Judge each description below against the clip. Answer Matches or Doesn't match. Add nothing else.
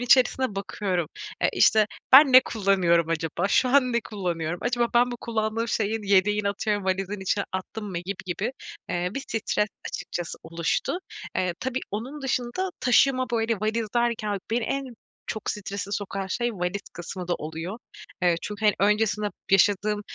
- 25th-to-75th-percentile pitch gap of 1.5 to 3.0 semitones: Doesn't match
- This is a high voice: Matches